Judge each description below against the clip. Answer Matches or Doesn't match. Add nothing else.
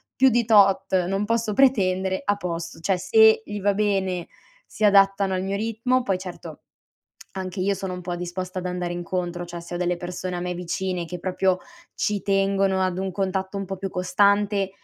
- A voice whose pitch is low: Doesn't match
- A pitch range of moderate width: Doesn't match